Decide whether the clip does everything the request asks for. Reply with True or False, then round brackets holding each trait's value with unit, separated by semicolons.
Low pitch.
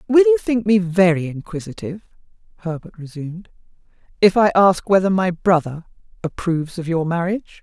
False (185 Hz)